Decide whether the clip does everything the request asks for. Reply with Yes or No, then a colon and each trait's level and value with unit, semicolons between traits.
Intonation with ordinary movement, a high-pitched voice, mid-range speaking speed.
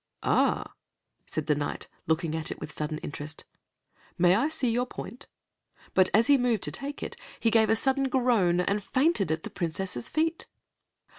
No: wide, 8.1 semitones; high, 210 Hz; average, 175 wpm